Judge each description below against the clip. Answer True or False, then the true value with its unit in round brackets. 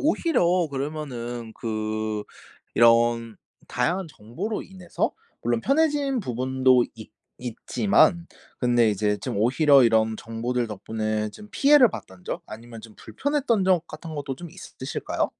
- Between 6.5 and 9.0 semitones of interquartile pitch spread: True (7.8 semitones)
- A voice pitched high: False (125 Hz)